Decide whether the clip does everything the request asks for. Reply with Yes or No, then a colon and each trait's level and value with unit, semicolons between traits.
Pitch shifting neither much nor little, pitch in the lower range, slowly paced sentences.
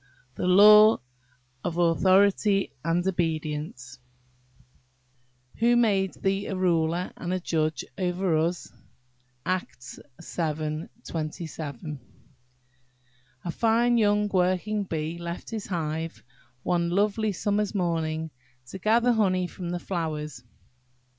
No: average, 3.9 semitones; medium, 175 Hz; slow, 100 wpm